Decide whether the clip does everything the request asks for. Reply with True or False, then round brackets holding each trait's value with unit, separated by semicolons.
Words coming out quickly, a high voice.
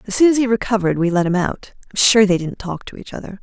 True (300 wpm; 200 Hz)